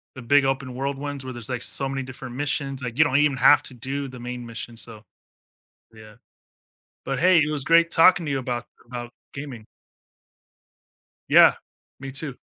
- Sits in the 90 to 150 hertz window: Yes, low, 135 Hz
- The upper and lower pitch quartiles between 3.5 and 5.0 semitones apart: No, narrow, 2.5 semitones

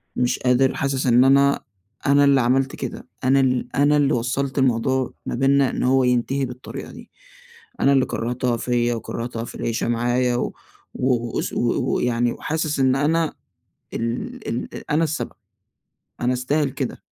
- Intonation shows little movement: Yes, narrow, 2.2 semitones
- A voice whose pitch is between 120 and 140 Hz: Yes, low, 130 Hz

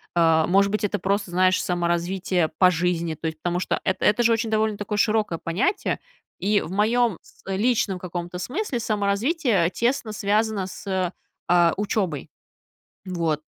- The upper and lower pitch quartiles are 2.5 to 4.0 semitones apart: Yes, average, 3.6 semitones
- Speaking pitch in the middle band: No, high, 195 Hz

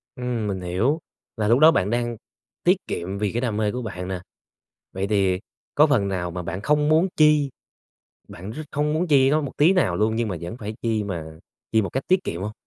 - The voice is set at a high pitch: No, low, 110 Hz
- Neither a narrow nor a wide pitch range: No, wide, 7.1 semitones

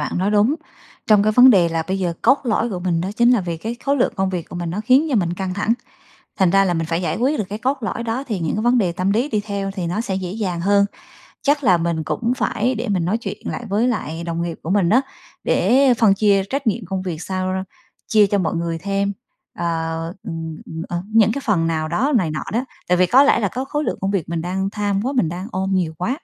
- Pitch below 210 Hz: Yes, high, 195 Hz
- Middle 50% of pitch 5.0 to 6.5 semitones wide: No, average, 4.6 semitones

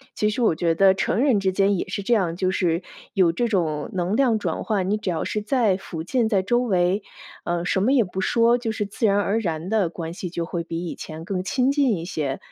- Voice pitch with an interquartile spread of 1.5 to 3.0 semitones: No, average, 4.2 semitones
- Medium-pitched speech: No, high, 195 Hz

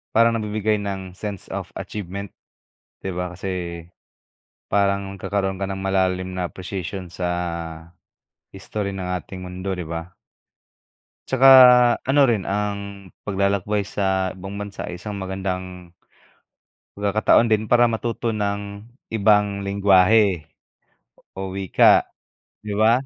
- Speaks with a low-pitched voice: Yes, low, 100 Hz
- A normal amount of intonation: No, narrow, 1.8 semitones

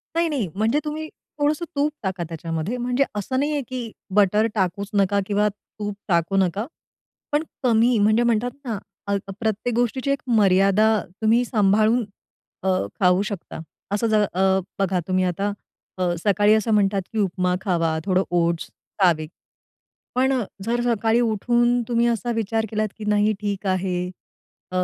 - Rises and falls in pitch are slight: No, average, 3.8 semitones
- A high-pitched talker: Yes, high, 210 Hz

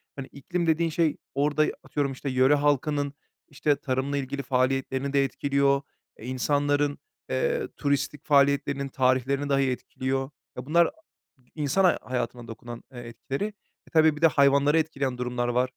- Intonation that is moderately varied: No, narrow, 2.1 semitones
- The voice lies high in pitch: No, medium, 140 Hz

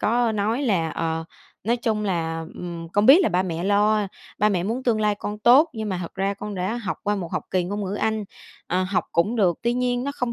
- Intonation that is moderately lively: Yes, average, 3.9 semitones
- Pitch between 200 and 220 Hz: Yes, high, 205 Hz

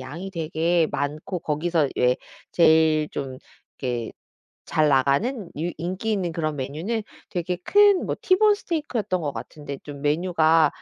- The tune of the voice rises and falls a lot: No, average, 4.1 semitones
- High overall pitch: No, medium, 165 Hz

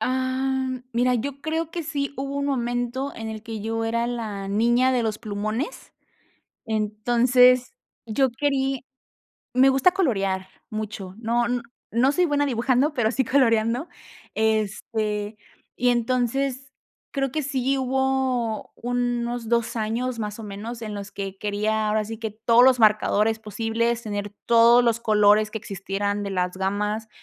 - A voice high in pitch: Yes, high, 235 Hz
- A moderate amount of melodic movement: Yes, average, 3.3 semitones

